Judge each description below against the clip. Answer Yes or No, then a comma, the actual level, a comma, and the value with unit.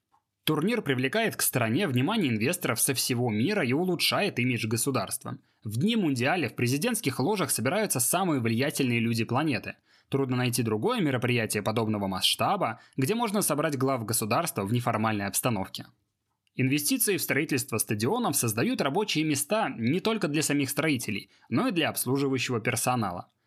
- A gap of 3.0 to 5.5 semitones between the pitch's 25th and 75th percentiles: Yes, average, 4.8 semitones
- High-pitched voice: No, low, 130 Hz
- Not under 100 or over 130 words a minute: No, average, 140 wpm